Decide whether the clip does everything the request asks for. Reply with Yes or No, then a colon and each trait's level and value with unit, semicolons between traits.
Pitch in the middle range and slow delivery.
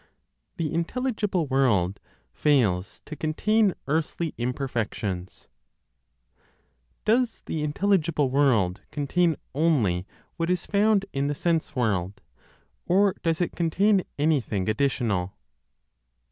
Yes: medium, 150 Hz; slow, 100 wpm